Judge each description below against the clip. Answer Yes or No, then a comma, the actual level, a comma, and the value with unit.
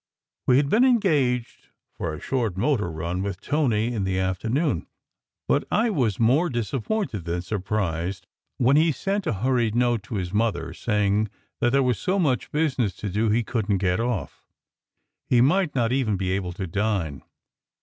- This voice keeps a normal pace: Yes, average, 175 wpm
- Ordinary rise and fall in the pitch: No, wide, 5.7 semitones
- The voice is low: Yes, low, 115 Hz